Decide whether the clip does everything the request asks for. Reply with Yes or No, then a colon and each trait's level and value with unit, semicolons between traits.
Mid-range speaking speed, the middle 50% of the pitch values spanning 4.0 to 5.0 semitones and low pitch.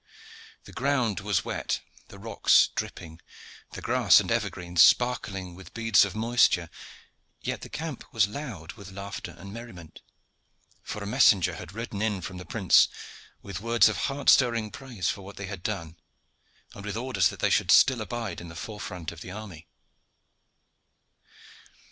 Yes: average, 165 wpm; average, 4.3 semitones; low, 100 Hz